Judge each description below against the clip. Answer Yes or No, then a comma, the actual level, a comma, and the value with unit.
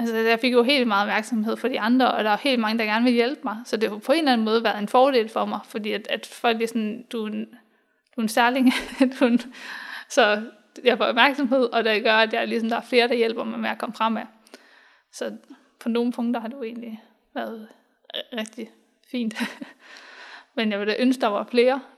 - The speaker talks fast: Yes, fast, 240 wpm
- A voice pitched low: No, high, 235 Hz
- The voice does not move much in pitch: Yes, narrow, 2.3 semitones